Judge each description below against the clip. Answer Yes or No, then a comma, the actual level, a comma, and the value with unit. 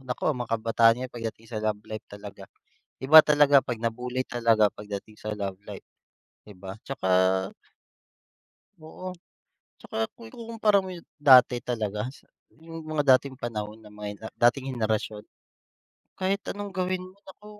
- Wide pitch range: Yes, wide, 6.4 semitones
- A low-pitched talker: Yes, low, 120 Hz